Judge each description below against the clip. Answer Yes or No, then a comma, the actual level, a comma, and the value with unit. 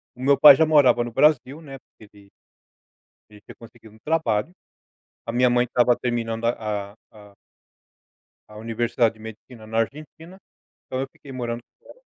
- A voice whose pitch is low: Yes, low, 120 Hz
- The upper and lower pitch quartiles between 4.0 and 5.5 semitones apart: No, average, 3.5 semitones